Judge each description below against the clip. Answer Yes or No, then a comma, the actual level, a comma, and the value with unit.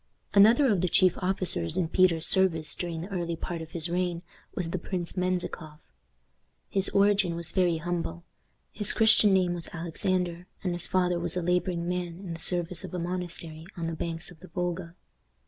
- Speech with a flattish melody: Yes, narrow, 1.6 semitones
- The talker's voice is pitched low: No, medium, 175 Hz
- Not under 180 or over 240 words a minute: Yes, average, 185 wpm